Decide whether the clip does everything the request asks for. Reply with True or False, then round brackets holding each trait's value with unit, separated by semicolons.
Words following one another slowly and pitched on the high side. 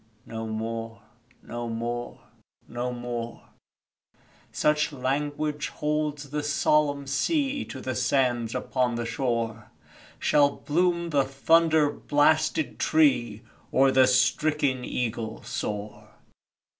False (105 wpm; 130 Hz)